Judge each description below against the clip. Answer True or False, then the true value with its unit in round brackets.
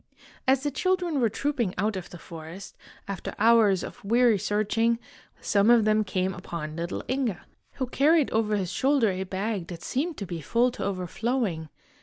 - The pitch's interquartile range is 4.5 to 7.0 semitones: True (5.1 semitones)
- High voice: True (215 Hz)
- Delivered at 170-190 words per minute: True (175 wpm)